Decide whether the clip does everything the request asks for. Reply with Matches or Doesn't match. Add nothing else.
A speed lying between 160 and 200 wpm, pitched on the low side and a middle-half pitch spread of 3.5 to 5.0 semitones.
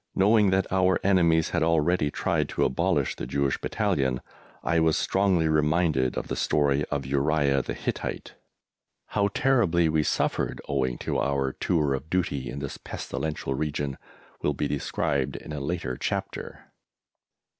Doesn't match